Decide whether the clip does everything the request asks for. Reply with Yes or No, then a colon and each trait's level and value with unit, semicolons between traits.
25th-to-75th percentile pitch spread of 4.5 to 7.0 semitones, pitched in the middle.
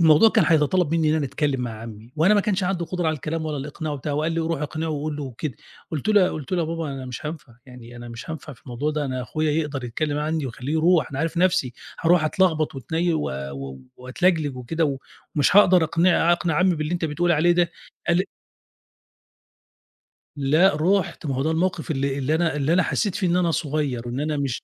No: average, 3.4 semitones; medium, 155 Hz